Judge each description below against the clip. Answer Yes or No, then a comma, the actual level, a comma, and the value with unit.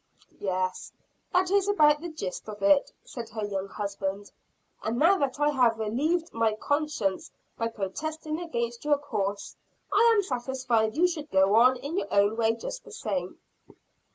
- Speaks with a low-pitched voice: No, high, 245 Hz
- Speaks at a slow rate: No, average, 165 wpm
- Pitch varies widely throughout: Yes, wide, 6.4 semitones